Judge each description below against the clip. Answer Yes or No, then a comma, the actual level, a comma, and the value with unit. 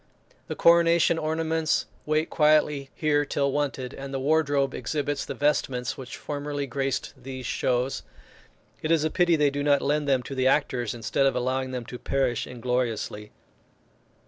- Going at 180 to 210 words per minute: No, average, 160 wpm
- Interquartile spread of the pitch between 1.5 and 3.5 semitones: Yes, average, 2.8 semitones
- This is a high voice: No, medium, 140 Hz